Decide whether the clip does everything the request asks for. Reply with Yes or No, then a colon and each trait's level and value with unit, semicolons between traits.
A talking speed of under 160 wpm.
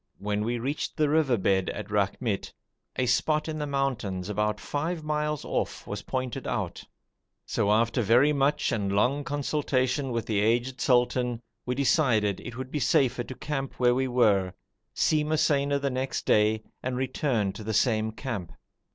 No: average, 165 wpm